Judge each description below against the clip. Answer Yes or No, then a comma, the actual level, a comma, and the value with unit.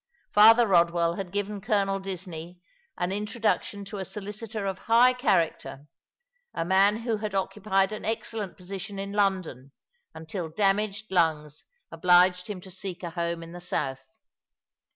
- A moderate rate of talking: Yes, average, 145 wpm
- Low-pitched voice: No, high, 195 Hz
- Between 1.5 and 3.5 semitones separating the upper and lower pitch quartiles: Yes, average, 3.1 semitones